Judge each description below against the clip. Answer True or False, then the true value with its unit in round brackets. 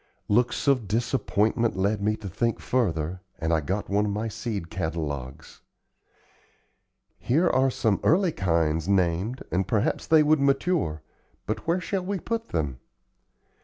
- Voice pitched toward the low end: True (105 Hz)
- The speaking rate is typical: True (145 wpm)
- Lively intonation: True (7.6 semitones)